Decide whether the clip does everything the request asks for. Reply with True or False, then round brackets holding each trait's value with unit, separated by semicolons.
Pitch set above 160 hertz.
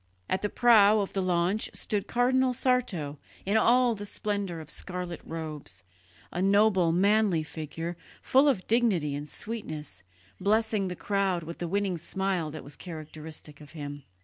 True (185 Hz)